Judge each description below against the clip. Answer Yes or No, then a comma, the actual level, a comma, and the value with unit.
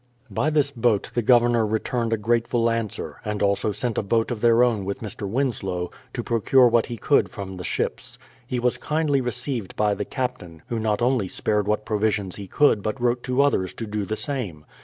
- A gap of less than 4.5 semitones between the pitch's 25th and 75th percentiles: Yes, average, 3.1 semitones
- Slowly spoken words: No, fast, 205 wpm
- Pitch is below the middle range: Yes, low, 115 Hz